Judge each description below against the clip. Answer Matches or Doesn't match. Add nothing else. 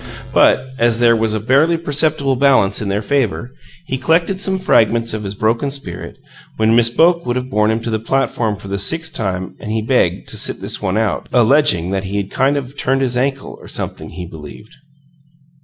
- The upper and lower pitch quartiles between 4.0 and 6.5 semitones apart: Matches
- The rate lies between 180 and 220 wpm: Matches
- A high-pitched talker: Doesn't match